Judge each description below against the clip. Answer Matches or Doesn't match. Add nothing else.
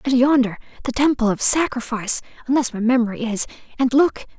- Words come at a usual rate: Matches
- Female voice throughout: Matches